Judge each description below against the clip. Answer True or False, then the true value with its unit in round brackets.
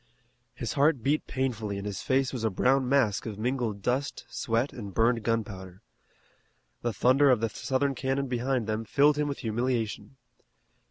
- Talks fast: False (165 wpm)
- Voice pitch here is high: False (120 Hz)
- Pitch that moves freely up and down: False (3.5 semitones)